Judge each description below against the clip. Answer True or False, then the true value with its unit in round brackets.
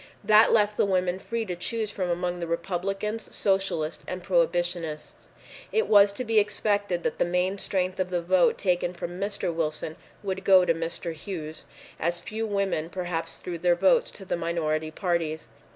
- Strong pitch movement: False (2.7 semitones)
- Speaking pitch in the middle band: True (180 Hz)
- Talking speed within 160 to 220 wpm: True (175 wpm)